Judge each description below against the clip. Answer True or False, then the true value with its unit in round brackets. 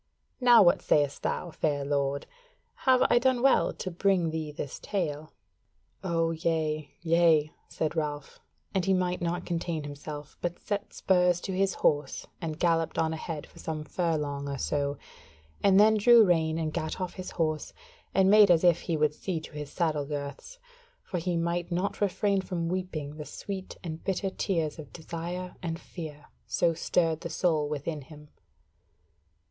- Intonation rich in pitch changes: False (3.2 semitones)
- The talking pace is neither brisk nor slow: True (170 wpm)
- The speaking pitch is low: False (165 Hz)